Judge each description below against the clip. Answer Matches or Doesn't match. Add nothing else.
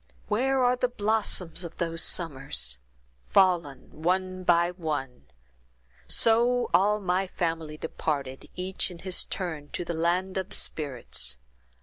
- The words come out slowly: Matches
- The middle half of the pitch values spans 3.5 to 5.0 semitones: Matches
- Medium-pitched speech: Matches